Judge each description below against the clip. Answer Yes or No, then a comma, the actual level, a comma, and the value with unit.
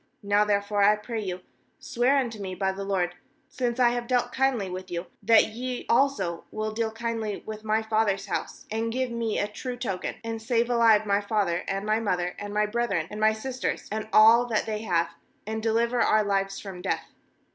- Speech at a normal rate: No, fast, 210 wpm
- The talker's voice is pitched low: No, high, 215 Hz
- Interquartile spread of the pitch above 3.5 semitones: No, average, 2.7 semitones